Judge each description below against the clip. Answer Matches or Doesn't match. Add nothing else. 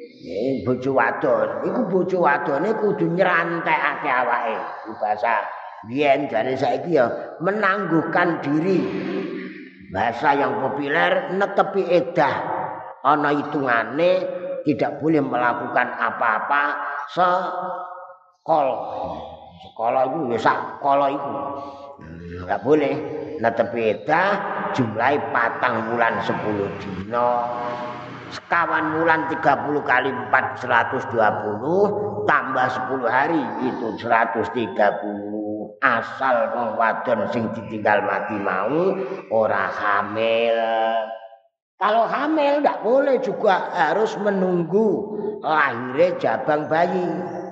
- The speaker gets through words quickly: Doesn't match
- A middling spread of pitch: Doesn't match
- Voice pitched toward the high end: Doesn't match